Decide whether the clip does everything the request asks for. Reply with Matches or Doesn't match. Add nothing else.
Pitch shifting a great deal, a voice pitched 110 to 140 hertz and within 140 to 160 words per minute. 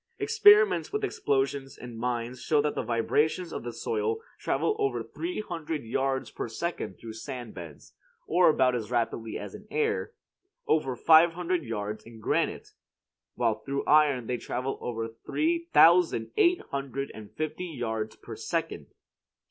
Matches